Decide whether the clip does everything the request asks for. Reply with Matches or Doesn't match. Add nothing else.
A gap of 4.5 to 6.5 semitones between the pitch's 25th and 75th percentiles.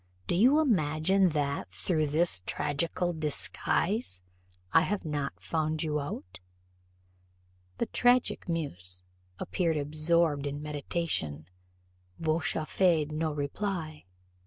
Doesn't match